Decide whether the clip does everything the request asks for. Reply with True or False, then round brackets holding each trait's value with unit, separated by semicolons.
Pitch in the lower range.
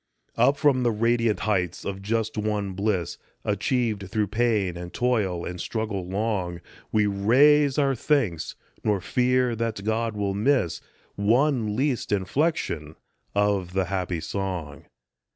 True (105 Hz)